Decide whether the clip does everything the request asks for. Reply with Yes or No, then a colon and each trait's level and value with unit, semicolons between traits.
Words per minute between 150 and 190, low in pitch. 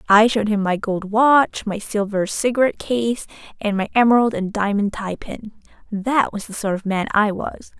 No: average, 185 wpm; high, 215 Hz